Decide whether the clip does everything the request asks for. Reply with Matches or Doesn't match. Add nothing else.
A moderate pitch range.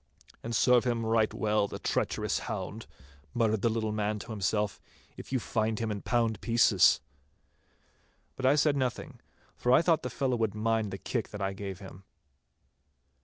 Doesn't match